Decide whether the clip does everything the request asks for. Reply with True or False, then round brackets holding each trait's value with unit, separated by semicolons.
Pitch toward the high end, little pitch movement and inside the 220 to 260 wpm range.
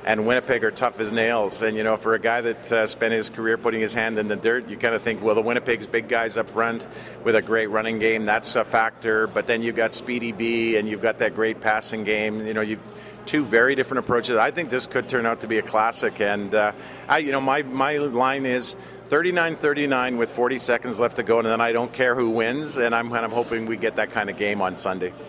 False (115 Hz; 1.7 semitones; 255 wpm)